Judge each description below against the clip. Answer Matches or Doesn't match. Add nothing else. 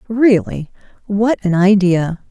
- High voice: Matches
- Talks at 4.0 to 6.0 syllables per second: Doesn't match